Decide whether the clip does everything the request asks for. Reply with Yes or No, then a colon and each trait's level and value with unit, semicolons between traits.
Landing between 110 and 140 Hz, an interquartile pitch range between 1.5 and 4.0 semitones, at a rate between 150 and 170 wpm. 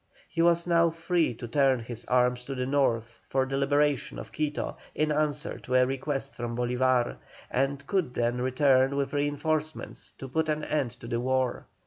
No: low, 135 Hz; average, 3.2 semitones; average, 180 wpm